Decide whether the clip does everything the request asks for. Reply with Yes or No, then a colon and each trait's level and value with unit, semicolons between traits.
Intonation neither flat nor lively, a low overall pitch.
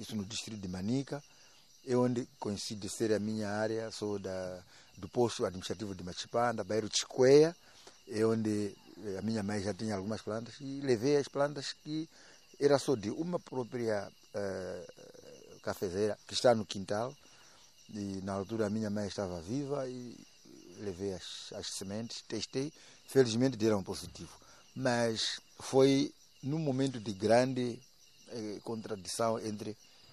Yes: average, 4.3 semitones; low, 110 Hz